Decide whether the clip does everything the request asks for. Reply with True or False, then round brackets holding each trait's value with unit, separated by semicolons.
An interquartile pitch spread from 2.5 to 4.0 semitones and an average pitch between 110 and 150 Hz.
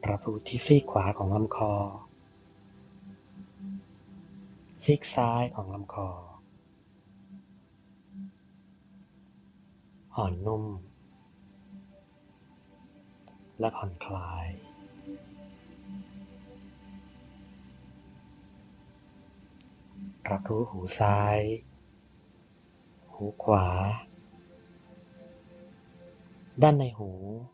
False (2.8 semitones; 100 Hz)